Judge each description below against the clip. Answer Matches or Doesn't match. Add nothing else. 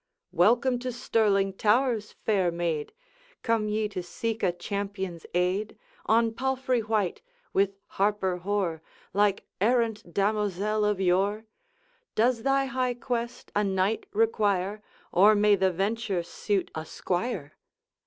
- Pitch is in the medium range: Doesn't match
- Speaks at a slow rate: Matches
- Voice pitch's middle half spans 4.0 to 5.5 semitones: Doesn't match